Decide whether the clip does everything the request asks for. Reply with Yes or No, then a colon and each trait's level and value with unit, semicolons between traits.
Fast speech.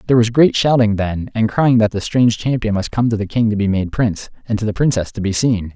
Yes: fast, 280 wpm